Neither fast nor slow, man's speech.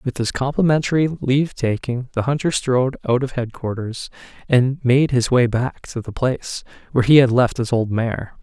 Yes: average, 190 wpm; male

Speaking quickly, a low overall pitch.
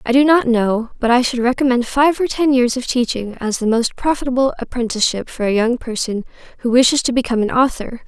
No: fast, 215 wpm; high, 245 Hz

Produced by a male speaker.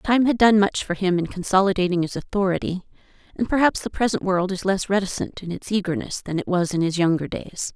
No: female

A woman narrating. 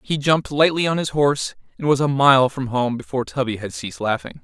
No: male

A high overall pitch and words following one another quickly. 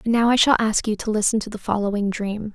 Yes: high, 215 Hz; fast, 285 wpm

